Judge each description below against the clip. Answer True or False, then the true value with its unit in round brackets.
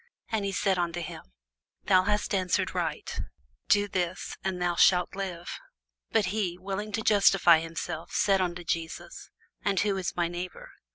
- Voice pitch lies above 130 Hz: True (185 Hz)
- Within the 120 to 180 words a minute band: True (160 wpm)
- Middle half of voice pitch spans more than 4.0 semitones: False (2.4 semitones)